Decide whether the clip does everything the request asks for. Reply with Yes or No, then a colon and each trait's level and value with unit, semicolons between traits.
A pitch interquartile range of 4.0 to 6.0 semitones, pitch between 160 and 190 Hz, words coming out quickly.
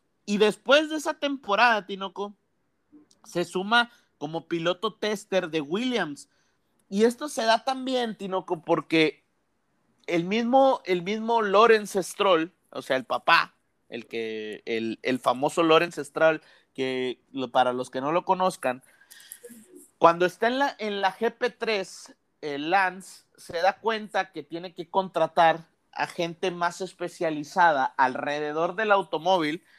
No: wide, 5.6 semitones; medium, 185 Hz; average, 135 wpm